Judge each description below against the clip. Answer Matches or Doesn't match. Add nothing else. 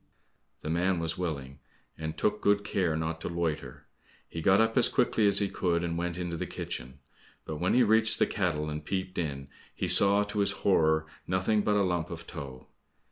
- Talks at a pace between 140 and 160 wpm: Doesn't match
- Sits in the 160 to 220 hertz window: Doesn't match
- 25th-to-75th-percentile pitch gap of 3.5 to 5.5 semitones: Matches